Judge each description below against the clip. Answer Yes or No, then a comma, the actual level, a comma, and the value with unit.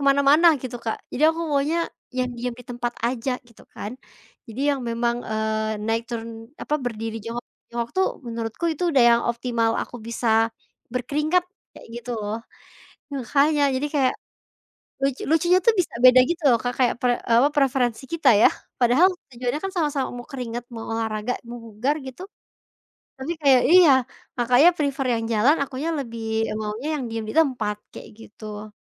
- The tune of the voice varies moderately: Yes, average, 3.6 semitones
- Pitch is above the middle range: Yes, high, 245 Hz